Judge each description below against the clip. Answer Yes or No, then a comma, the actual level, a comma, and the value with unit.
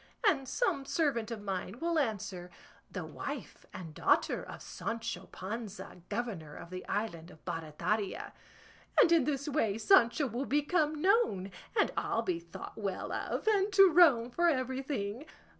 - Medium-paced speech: Yes, average, 150 wpm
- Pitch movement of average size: No, wide, 7.6 semitones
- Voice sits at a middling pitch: No, high, 235 Hz